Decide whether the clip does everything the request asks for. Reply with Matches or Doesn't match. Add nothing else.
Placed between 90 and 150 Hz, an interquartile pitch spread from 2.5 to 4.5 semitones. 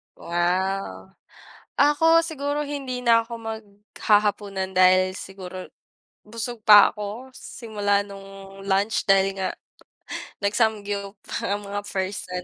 Doesn't match